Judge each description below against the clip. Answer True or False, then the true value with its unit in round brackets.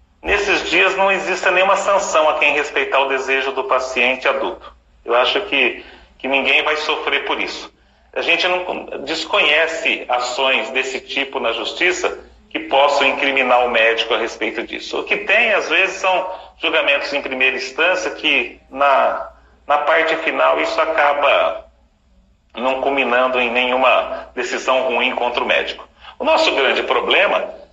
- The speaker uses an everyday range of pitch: False (6.0 semitones)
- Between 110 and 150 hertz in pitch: True (140 Hz)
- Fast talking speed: False (150 wpm)